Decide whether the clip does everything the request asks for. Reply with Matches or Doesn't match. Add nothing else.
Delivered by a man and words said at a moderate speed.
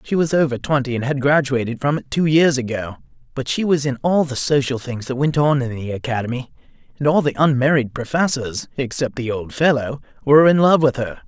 Doesn't match